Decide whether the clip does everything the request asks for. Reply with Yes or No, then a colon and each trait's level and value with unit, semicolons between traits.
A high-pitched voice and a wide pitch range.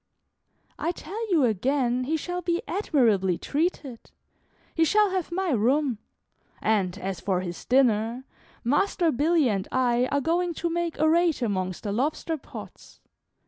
Yes: very high, 275 Hz; wide, 7.3 semitones